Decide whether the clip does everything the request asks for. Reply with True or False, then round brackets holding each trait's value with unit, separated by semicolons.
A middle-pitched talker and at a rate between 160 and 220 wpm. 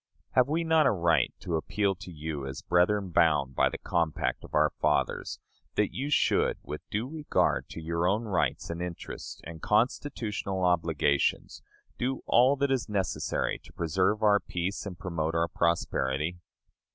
False (90 Hz; 165 wpm)